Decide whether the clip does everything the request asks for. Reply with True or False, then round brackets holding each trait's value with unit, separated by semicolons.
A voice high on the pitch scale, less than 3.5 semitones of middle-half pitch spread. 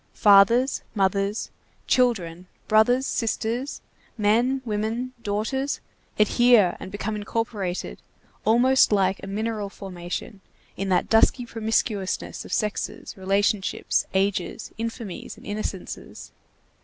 True (215 Hz; 2.9 semitones)